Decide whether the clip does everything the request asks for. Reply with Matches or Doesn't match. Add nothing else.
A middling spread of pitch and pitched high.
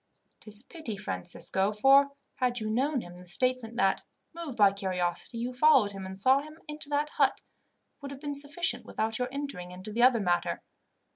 Doesn't match